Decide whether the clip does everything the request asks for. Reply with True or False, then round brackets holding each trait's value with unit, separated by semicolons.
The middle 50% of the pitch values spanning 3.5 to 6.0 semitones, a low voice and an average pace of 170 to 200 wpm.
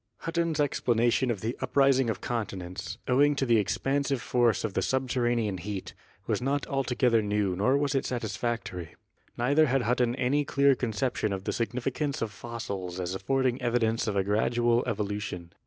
False (4.2 semitones; 120 Hz; 160 wpm)